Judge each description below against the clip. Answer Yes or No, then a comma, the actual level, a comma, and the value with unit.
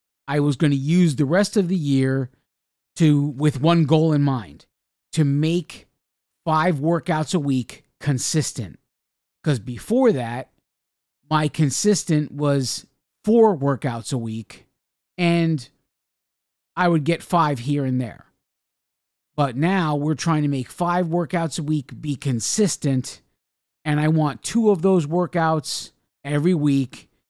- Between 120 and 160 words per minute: Yes, slow, 135 wpm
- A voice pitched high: No, medium, 155 Hz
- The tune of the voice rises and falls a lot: No, average, 3.4 semitones